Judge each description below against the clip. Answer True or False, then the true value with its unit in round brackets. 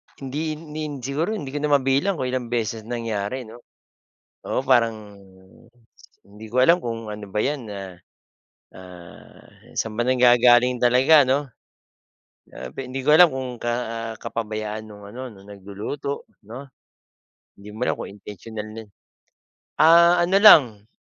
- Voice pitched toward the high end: False (120 Hz)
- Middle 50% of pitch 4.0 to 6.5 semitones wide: True (4.4 semitones)